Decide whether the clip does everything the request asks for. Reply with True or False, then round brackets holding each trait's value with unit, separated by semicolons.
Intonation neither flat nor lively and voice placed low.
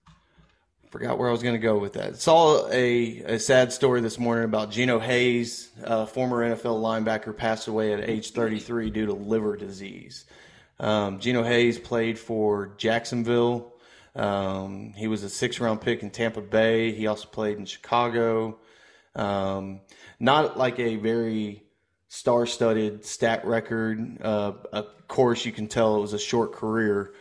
False (1.9 semitones; 110 Hz)